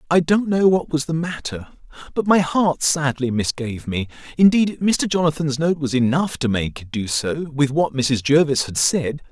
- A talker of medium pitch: Yes, medium, 145 Hz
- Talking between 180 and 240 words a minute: Yes, average, 195 wpm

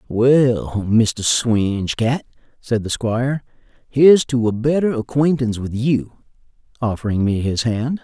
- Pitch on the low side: Yes, low, 120 Hz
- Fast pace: No, slow, 135 wpm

